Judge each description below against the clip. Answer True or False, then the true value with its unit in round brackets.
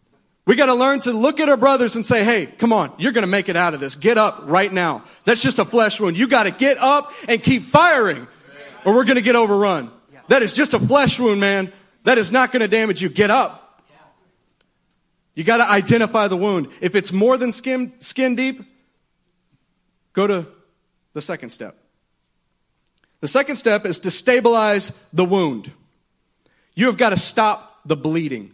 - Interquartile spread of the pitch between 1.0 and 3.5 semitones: False (4.9 semitones)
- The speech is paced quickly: False (185 wpm)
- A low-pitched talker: False (215 Hz)